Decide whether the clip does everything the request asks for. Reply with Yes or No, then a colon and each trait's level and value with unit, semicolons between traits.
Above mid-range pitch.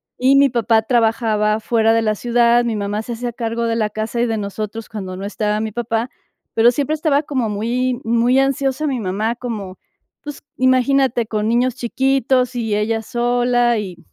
Yes: high, 235 Hz